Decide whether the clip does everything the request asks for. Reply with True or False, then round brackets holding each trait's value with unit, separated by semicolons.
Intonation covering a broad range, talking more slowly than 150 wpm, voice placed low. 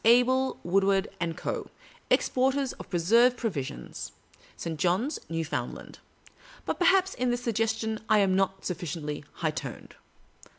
False (6.3 semitones; 135 wpm; 200 Hz)